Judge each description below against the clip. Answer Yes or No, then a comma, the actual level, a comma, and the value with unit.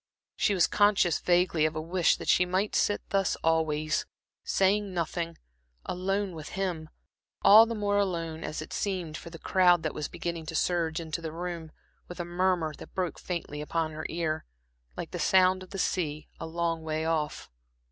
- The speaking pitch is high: No, medium, 170 Hz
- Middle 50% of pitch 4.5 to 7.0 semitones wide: No, average, 2.7 semitones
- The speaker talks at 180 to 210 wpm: Yes, average, 185 wpm